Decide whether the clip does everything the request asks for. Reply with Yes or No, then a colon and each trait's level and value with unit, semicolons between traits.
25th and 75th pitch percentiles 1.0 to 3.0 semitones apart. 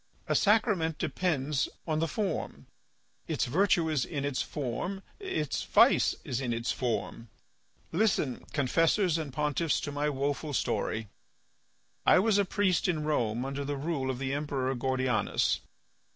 No: average, 4.3 semitones